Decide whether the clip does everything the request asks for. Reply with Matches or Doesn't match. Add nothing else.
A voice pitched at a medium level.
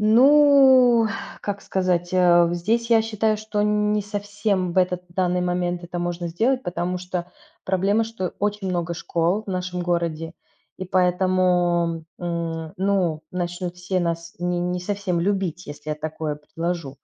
Matches